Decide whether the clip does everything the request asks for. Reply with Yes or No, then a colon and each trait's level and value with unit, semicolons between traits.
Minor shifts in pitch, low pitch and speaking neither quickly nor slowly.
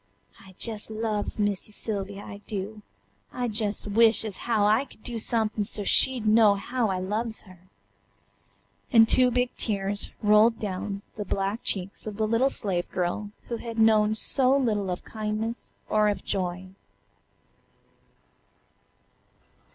No: narrow, 2.1 semitones; high, 215 Hz; average, 145 wpm